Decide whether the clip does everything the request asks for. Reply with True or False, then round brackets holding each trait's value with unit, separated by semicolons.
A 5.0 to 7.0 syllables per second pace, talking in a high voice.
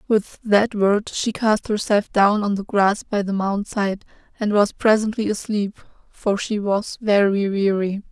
False (4.0 syllables/s; 205 Hz)